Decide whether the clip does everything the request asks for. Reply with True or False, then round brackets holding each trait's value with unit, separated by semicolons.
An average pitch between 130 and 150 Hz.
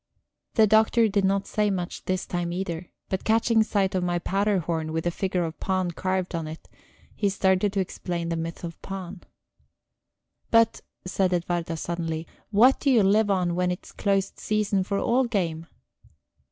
False (185 Hz)